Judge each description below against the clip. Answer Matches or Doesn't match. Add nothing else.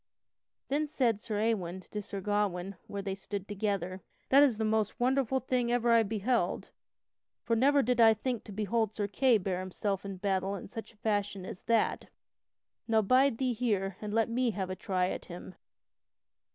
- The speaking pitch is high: Matches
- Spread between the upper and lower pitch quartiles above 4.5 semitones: Doesn't match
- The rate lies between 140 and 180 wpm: Doesn't match